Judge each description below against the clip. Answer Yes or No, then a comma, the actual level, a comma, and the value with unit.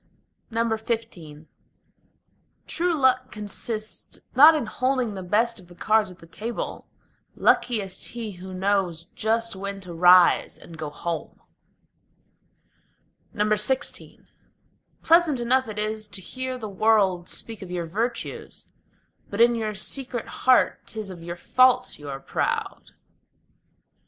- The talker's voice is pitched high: Yes, high, 215 Hz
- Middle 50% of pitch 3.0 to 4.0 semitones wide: No, average, 4.5 semitones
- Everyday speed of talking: No, slow, 125 wpm